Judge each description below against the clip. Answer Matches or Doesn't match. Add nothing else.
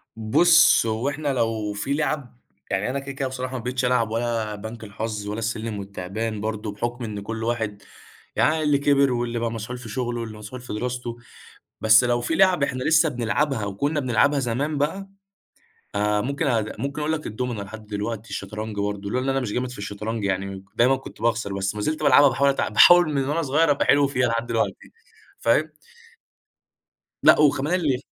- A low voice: Matches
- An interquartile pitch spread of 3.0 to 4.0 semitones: Doesn't match